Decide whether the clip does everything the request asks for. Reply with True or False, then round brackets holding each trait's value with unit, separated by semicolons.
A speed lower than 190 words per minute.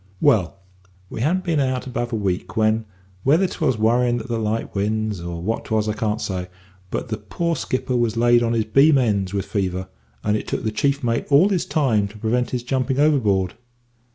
False (205 wpm)